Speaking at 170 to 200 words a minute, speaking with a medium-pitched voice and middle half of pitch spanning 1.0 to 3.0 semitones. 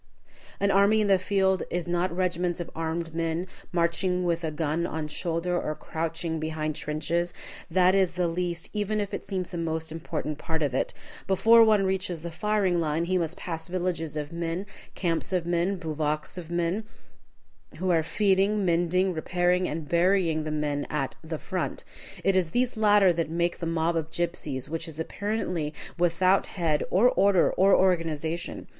Yes: average, 175 wpm; medium, 170 Hz; narrow, 2.6 semitones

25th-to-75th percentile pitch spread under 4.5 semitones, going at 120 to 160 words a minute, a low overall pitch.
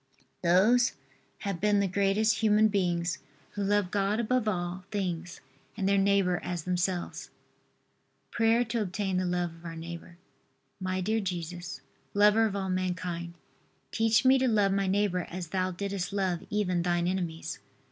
No: average, 2.7 semitones; average, 155 wpm; high, 190 Hz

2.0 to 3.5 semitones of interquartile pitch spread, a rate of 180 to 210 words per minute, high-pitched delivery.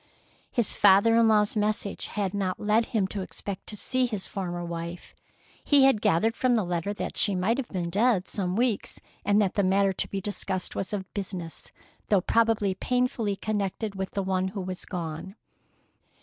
Yes: average, 2.7 semitones; average, 185 wpm; high, 200 Hz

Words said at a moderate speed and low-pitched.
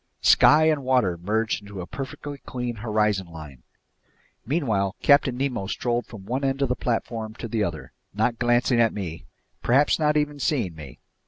Yes: average, 170 wpm; low, 115 Hz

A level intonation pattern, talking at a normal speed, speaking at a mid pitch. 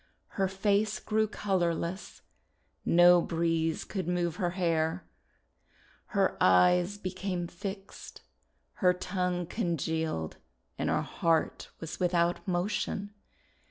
No: narrow, 2.3 semitones; slow, 105 wpm; medium, 180 Hz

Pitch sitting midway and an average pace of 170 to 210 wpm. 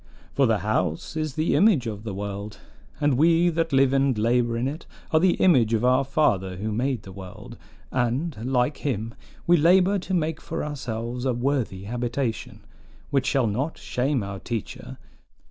No: low, 125 Hz; average, 175 wpm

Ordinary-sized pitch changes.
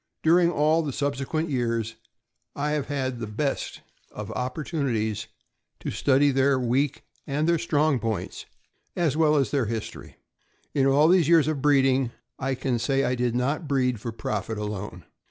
Yes: average, 4.0 semitones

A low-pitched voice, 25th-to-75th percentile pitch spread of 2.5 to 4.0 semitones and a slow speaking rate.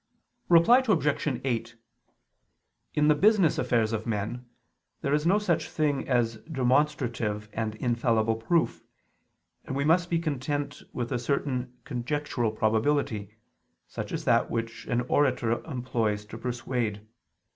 No: low, 125 Hz; average, 4.5 semitones; slow, 130 wpm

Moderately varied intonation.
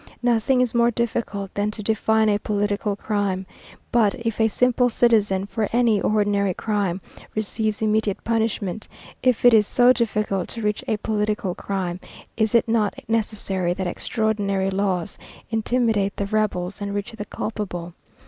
No: narrow, 2.1 semitones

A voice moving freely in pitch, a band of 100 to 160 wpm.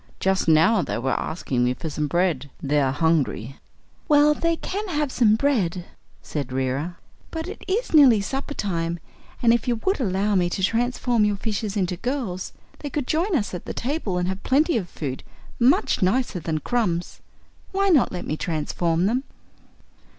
No: wide, 8.0 semitones; average, 180 wpm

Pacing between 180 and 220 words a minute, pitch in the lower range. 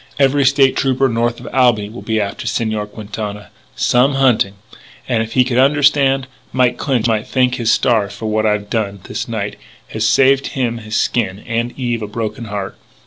Yes: average, 185 wpm; low, 115 Hz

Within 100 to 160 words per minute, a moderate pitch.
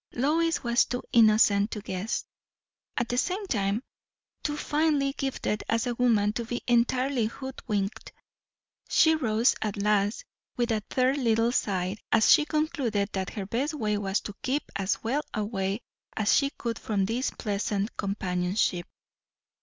No: average, 150 wpm; high, 230 Hz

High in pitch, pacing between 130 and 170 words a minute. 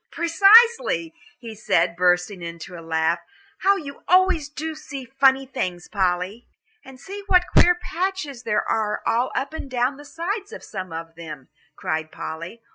Yes: very high, 255 Hz; average, 160 wpm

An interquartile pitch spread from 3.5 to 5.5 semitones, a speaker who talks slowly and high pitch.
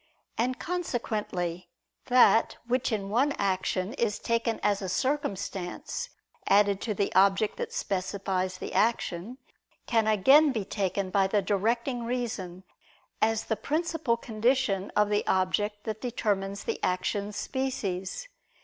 Yes: average, 4.0 semitones; slow, 130 wpm; high, 210 Hz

